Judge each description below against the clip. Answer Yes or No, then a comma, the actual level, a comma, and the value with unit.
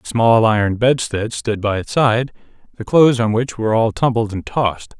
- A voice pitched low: Yes, low, 115 Hz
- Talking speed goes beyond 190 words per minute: Yes, fast, 205 wpm